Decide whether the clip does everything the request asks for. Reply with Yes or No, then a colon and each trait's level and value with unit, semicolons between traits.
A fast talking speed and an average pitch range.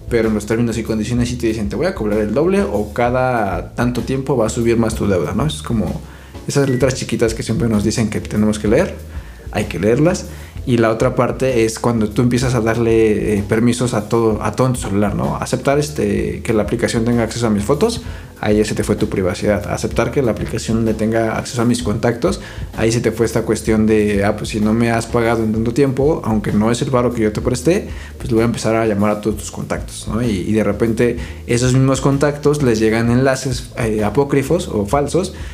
No: fast, 235 wpm; narrow, 2.3 semitones